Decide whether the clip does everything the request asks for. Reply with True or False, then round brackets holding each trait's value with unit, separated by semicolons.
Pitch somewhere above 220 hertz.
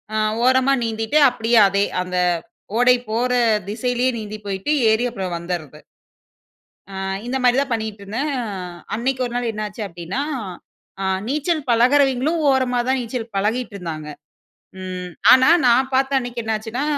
True (235 Hz)